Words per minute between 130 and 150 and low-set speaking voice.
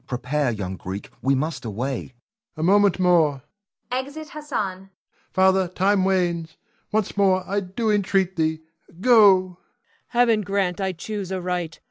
No: average, 140 wpm; medium, 185 Hz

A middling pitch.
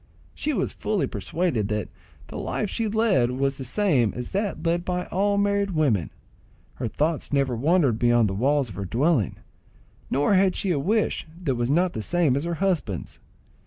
Yes: medium, 150 Hz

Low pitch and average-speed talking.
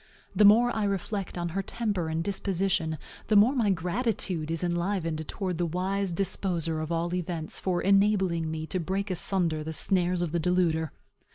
No: medium, 180 Hz; average, 175 wpm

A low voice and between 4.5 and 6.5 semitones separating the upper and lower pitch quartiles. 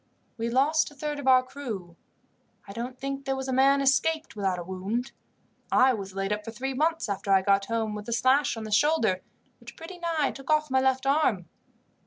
No: very high, 255 Hz; average, 5.1 semitones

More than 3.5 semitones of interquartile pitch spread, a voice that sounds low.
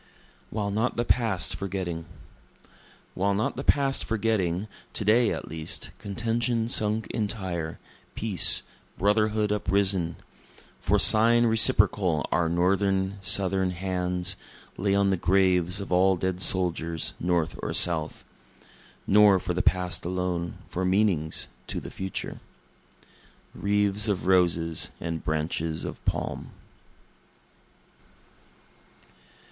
No: average, 3.0 semitones; very low, 95 Hz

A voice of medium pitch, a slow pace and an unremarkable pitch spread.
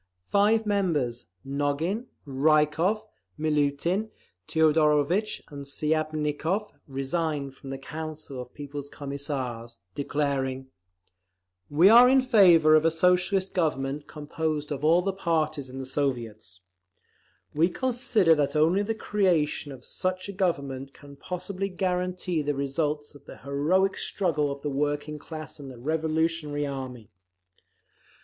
Yes: medium, 150 Hz; slow, 120 wpm; average, 4.3 semitones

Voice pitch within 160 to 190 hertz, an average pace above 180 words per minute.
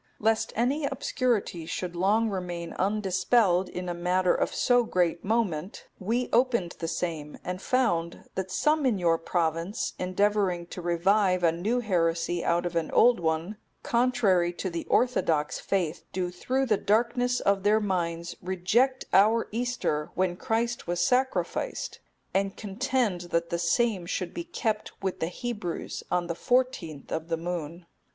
No: medium, 185 Hz; average, 155 wpm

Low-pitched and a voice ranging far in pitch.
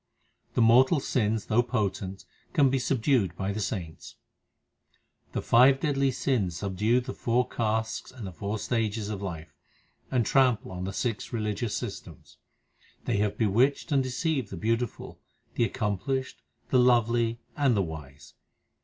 No: low, 115 Hz; average, 4.2 semitones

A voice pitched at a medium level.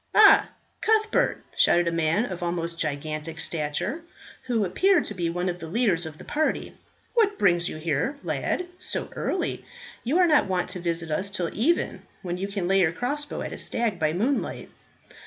Yes: medium, 180 Hz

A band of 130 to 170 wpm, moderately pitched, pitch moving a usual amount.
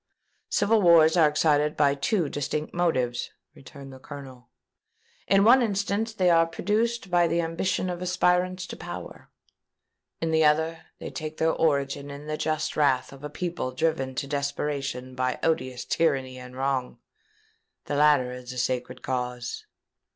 Yes: average, 155 wpm; medium, 150 Hz; average, 4.5 semitones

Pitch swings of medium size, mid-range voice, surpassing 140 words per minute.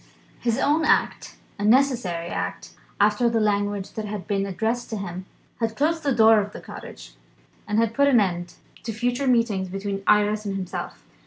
No: average, 3.3 semitones; high, 210 Hz; average, 180 wpm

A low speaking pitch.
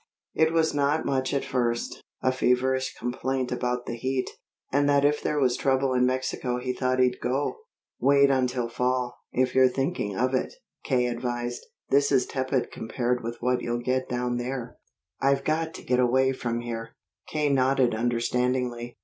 Yes: low, 130 Hz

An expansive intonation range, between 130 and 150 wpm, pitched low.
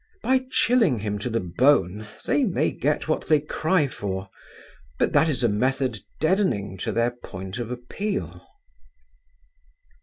Yes: wide, 7.4 semitones; average, 145 wpm; low, 125 Hz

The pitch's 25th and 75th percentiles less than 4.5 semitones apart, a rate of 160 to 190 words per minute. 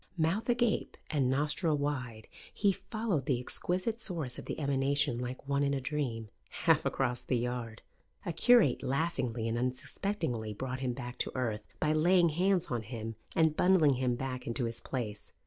No: average, 5.0 semitones; average, 170 wpm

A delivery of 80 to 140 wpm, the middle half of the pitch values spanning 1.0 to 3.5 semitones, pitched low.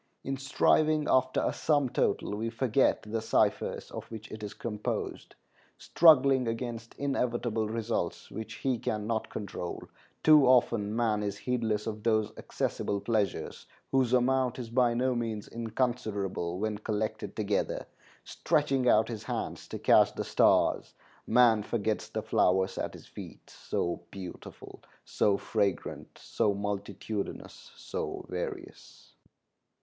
Yes: slow, 135 wpm; average, 3.1 semitones; low, 115 Hz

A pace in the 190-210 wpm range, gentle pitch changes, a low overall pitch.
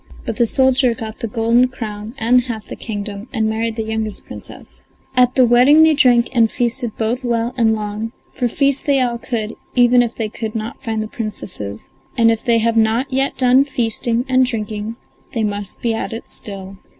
No: average, 200 wpm; narrow, 2.2 semitones; high, 230 Hz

